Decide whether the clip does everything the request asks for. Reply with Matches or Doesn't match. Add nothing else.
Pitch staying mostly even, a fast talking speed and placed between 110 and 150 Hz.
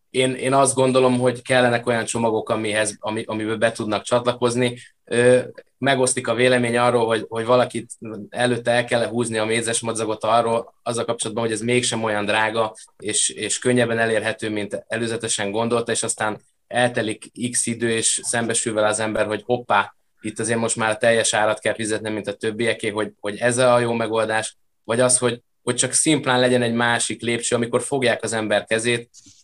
Matches